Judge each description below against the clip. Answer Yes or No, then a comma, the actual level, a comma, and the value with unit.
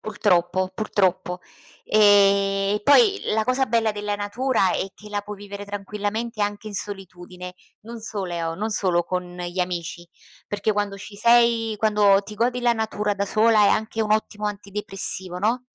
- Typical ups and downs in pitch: No, narrow, 2.2 semitones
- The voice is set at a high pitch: Yes, high, 205 Hz